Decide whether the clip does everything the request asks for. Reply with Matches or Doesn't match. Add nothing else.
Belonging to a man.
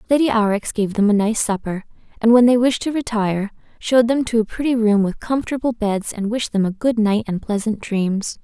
Doesn't match